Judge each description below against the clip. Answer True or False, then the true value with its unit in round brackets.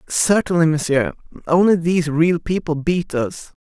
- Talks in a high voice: False (165 Hz)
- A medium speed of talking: False (130 wpm)